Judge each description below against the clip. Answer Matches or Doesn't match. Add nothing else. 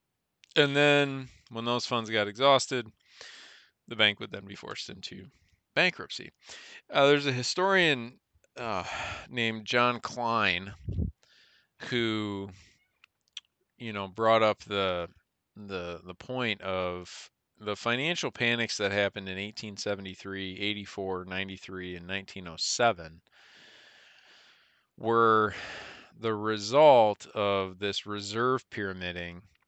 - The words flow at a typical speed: Doesn't match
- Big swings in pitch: Doesn't match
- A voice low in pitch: Matches